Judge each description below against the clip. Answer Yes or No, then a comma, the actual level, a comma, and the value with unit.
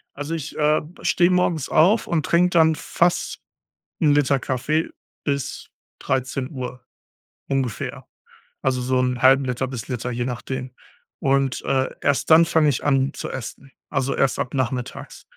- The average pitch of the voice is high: No, low, 135 Hz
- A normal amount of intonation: Yes, average, 3.2 semitones